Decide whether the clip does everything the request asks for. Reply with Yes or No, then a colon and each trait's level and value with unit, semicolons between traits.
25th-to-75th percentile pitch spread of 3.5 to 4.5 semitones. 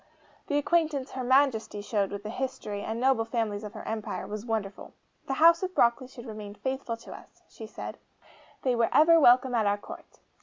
Yes: average, 3.9 semitones